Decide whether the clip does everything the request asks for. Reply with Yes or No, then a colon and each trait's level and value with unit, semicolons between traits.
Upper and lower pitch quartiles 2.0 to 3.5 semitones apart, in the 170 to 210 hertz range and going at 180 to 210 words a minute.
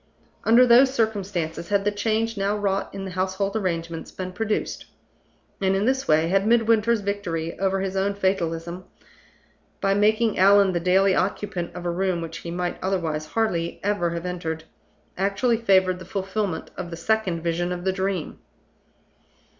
No: average, 2.9 semitones; high, 190 Hz; average, 160 wpm